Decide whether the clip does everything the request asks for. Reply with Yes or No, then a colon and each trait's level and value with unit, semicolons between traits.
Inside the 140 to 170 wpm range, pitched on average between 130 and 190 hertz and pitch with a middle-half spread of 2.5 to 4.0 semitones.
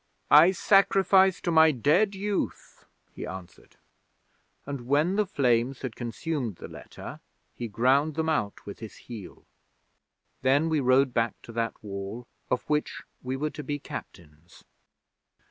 No: average, 145 wpm; low, 135 Hz; wide, 5.5 semitones